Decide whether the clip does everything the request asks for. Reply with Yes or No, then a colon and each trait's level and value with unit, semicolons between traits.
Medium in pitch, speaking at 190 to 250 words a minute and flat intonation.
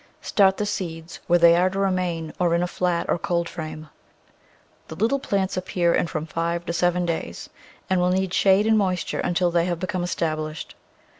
Yes: medium, 175 Hz; average, 195 wpm; narrow, 1.9 semitones